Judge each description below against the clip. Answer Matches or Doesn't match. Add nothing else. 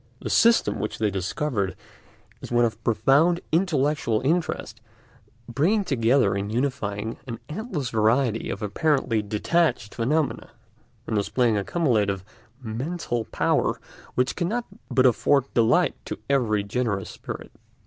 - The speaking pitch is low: Matches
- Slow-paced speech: Matches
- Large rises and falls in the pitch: Matches